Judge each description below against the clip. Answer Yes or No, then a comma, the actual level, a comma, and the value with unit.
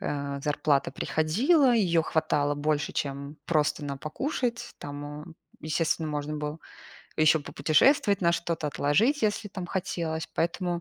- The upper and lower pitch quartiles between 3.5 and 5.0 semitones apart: Yes, average, 3.8 semitones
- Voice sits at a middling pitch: Yes, medium, 155 Hz